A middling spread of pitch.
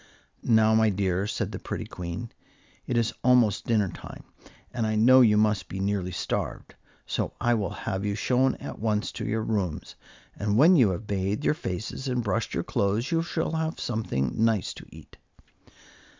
Yes: average, 3.4 semitones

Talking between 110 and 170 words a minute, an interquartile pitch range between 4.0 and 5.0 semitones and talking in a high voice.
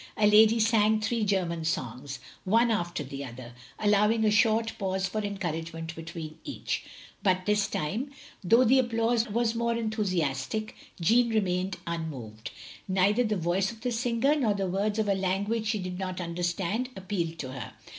Yes: average, 165 wpm; average, 4.7 semitones; high, 200 Hz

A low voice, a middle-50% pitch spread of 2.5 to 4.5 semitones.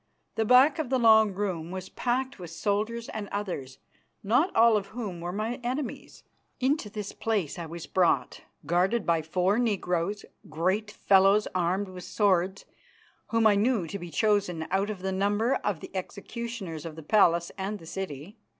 No: high, 200 Hz; average, 3.8 semitones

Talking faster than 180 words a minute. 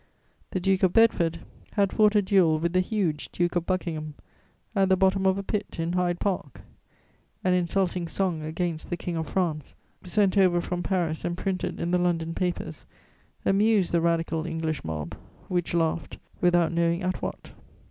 No: average, 175 wpm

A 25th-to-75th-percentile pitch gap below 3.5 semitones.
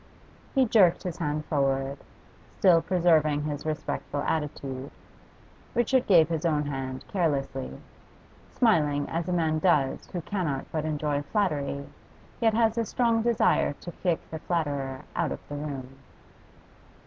No: average, 4.0 semitones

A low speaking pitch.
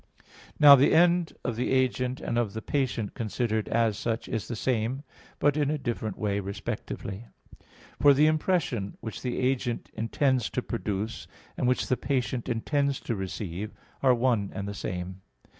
Yes: low, 120 Hz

